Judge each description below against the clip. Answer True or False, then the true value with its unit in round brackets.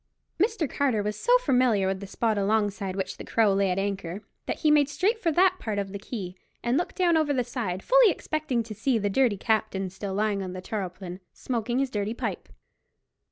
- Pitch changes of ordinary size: False (6.2 semitones)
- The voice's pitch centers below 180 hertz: False (220 Hz)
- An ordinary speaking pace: False (210 wpm)